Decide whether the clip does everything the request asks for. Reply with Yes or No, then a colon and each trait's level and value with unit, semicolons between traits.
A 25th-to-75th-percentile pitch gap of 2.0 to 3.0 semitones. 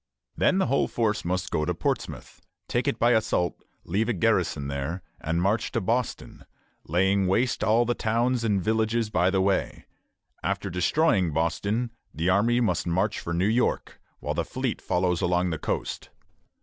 No: average, 4.6 semitones